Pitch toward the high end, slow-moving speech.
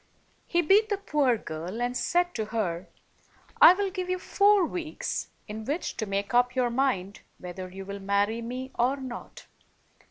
No: high, 245 Hz; average, 170 wpm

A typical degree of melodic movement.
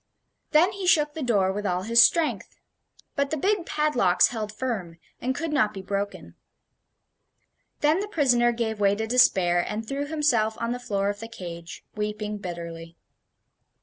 No: wide, 6.4 semitones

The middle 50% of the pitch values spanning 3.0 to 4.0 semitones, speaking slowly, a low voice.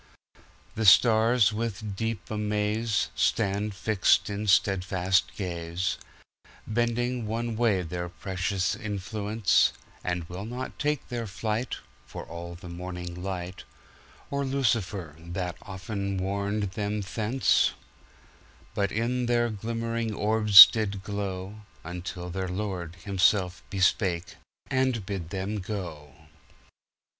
Yes: average, 3.3 semitones; slow, 95 wpm; low, 100 Hz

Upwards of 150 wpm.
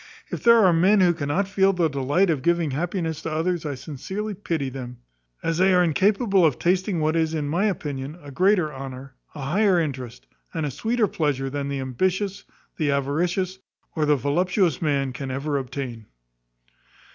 Yes: average, 180 wpm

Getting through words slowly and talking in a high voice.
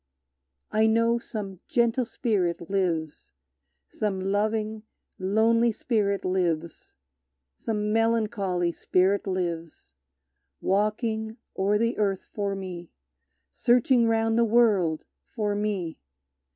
Yes: slow, 100 wpm; high, 210 Hz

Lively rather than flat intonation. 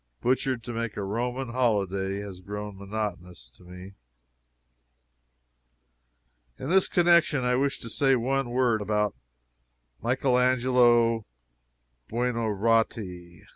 No: average, 4.0 semitones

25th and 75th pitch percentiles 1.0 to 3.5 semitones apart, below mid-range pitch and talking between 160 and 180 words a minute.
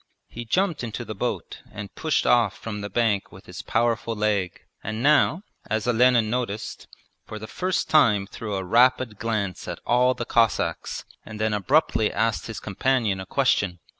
Yes: average, 3.0 semitones; low, 110 Hz; average, 170 wpm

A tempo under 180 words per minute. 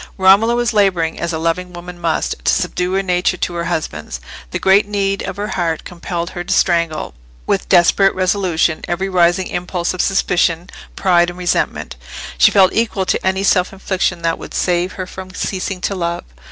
No: average, 185 wpm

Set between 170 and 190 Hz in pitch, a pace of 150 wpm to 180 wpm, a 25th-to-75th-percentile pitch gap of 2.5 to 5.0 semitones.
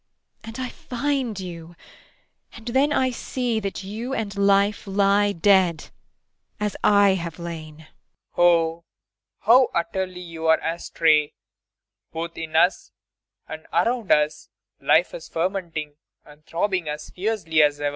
No: medium, 185 Hz; slow, 135 wpm; average, 4.5 semitones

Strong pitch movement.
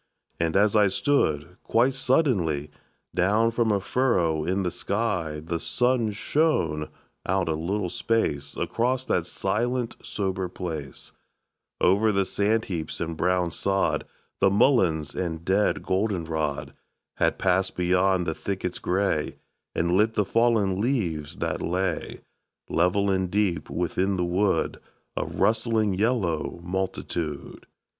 No: average, 4.3 semitones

